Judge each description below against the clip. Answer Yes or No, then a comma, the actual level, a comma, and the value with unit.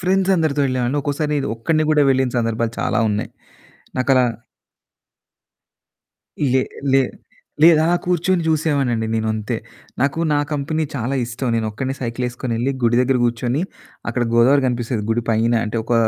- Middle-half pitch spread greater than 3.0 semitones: Yes, average, 4.1 semitones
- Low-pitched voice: Yes, low, 130 Hz